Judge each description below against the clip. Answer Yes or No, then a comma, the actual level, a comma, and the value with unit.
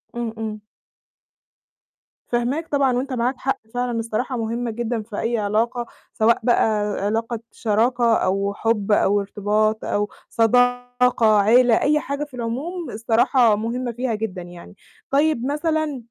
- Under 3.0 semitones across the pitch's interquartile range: Yes, narrow, 2.5 semitones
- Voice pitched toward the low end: No, high, 235 Hz